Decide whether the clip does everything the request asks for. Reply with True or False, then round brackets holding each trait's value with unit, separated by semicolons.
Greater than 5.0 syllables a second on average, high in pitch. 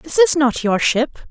False (3.9 syllables/s; 280 Hz)